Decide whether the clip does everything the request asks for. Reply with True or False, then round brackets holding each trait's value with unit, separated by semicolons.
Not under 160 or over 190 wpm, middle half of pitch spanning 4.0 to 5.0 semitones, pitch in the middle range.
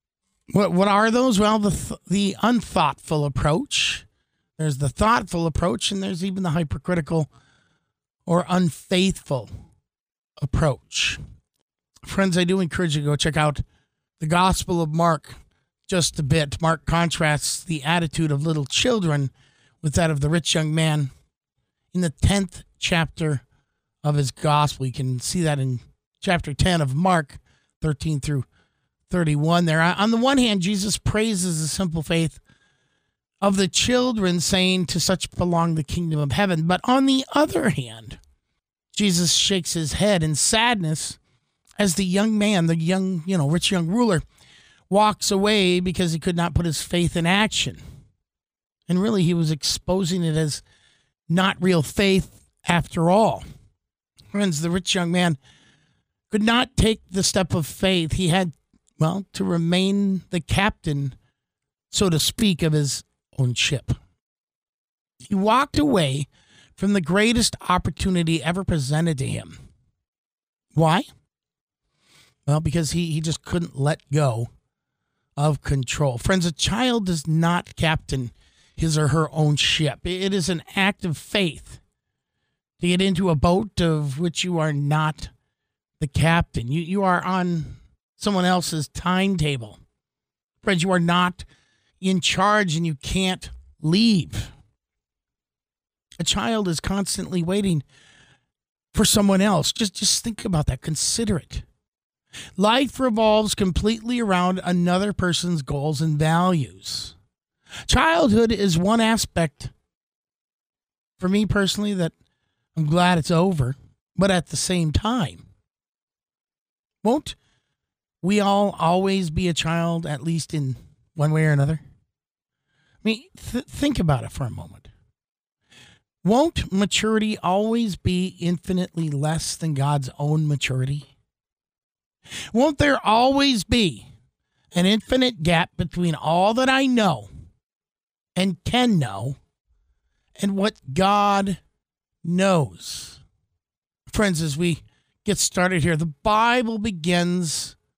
False (135 wpm; 4.6 semitones; 170 Hz)